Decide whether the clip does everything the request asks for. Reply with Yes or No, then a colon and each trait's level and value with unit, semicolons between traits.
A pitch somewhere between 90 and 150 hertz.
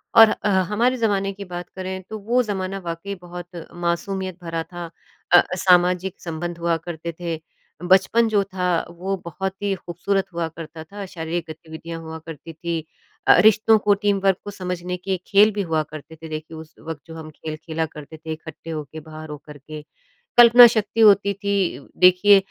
No: medium, 175 Hz